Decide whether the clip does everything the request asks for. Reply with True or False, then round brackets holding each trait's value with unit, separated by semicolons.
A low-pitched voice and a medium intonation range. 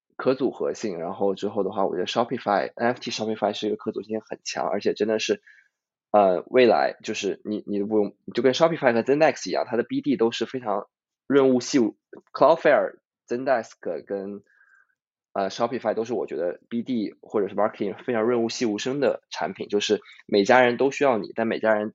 True (115 Hz; 4.3 semitones)